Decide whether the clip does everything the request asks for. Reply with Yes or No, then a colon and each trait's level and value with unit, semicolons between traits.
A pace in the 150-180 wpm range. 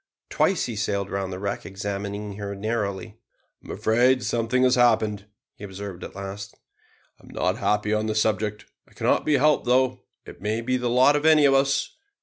No: average, 195 wpm